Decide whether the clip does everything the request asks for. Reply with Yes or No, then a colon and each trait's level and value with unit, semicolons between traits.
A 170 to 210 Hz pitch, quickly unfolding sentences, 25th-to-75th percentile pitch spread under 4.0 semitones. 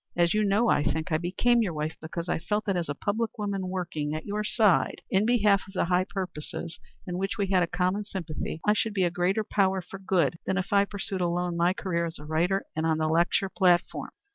Yes: medium, 185 Hz; fast, 240 wpm; average, 2.9 semitones